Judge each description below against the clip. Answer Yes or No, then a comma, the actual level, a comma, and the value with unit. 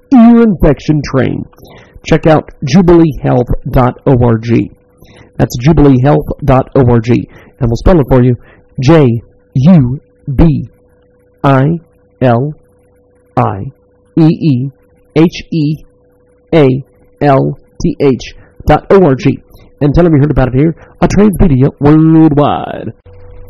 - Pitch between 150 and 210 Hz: No, low, 135 Hz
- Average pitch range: No, wide, 7.5 semitones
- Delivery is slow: Yes, slow, 70 wpm